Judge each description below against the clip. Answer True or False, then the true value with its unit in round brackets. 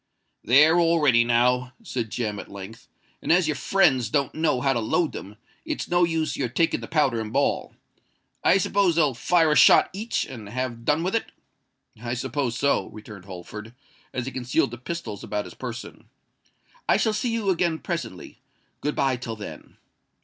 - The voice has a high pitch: False (130 Hz)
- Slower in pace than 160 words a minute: False (185 wpm)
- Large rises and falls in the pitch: True (6.0 semitones)